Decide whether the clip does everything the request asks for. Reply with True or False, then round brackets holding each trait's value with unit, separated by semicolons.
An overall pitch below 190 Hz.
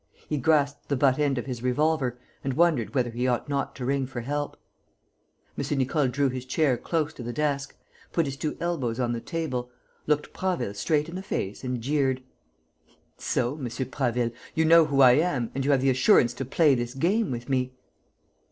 True (135 Hz)